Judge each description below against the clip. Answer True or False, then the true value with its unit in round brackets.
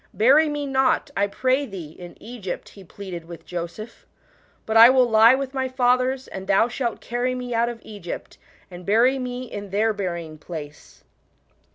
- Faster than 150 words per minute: True (190 wpm)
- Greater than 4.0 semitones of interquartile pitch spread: True (5.1 semitones)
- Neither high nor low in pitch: False (225 Hz)